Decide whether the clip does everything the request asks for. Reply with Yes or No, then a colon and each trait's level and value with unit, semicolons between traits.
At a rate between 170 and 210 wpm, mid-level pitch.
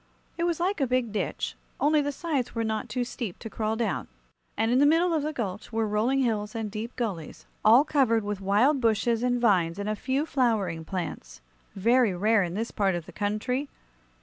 No: fast, 205 wpm; high, 230 Hz